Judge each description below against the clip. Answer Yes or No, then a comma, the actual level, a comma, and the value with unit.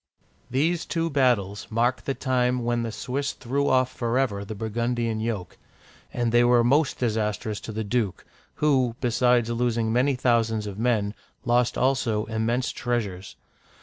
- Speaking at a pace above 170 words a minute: No, average, 150 wpm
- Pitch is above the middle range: No, low, 120 Hz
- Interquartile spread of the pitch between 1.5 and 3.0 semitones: Yes, narrow, 2.4 semitones